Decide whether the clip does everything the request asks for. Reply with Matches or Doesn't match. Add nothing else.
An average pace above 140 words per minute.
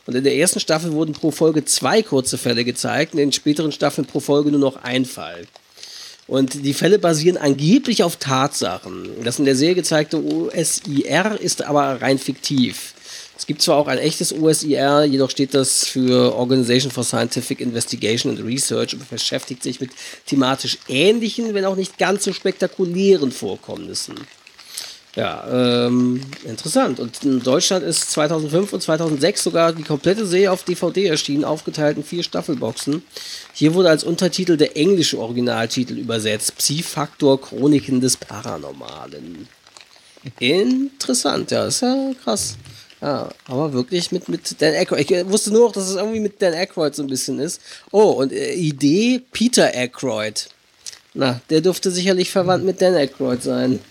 Matches